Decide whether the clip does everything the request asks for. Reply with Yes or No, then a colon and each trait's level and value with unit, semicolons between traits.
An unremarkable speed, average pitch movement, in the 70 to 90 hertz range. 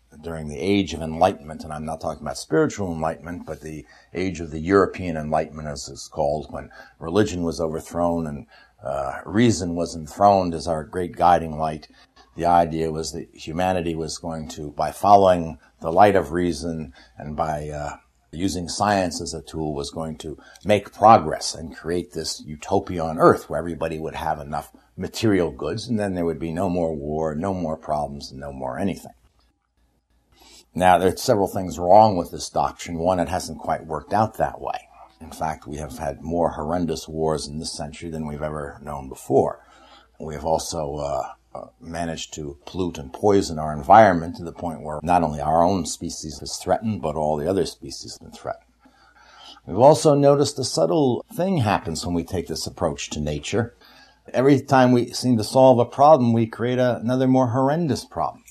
Yes: average, 185 wpm; average, 3.5 semitones; very low, 85 Hz